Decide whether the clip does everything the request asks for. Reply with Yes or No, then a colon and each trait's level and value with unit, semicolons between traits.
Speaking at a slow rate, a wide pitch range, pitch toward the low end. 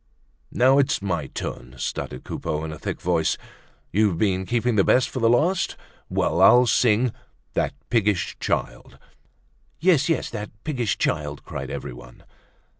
No: average, 150 wpm; wide, 6.7 semitones; low, 105 Hz